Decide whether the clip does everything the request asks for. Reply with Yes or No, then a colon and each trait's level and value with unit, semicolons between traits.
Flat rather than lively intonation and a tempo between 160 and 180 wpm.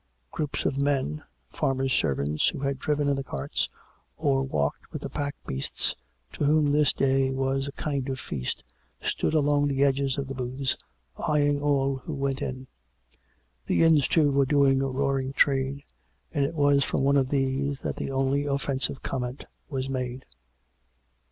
Yes: narrow, 1.3 semitones; average, 175 wpm